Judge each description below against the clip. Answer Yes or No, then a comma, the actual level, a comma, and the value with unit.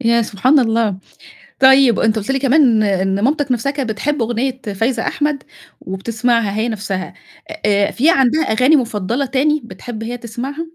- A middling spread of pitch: Yes, average, 3.8 semitones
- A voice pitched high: Yes, high, 235 Hz